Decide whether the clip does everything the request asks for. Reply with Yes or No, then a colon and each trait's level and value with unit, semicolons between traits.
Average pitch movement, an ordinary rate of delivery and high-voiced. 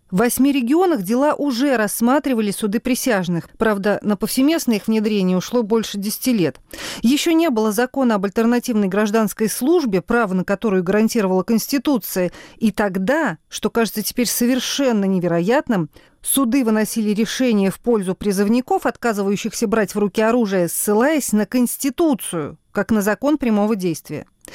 Yes: average, 3.7 semitones; average, 135 wpm; high, 225 Hz